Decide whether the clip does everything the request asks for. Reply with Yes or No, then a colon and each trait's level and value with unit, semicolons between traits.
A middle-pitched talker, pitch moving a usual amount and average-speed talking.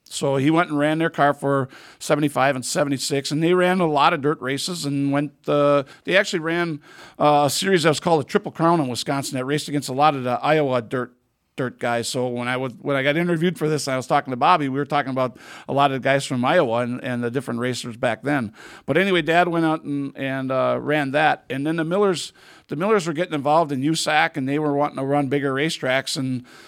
No: medium, 145 Hz; average, 3.1 semitones; fast, 245 wpm